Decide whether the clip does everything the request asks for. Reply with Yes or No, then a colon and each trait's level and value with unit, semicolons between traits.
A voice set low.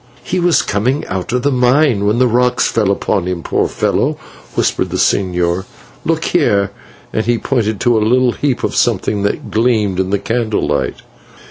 Yes: low, 110 Hz